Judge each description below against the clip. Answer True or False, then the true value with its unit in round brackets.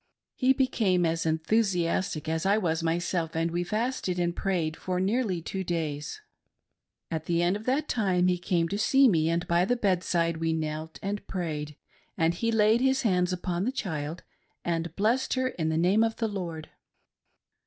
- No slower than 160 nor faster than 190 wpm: True (180 wpm)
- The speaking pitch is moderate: True (180 Hz)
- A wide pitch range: False (4.4 semitones)